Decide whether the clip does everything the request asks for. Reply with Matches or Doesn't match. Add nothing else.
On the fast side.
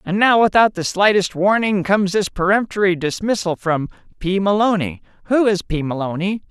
Doesn't match